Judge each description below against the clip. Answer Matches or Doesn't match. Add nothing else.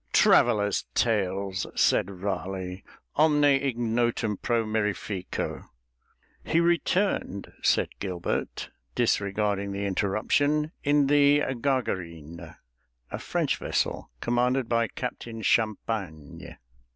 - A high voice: Doesn't match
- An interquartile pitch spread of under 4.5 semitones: Doesn't match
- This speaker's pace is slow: Matches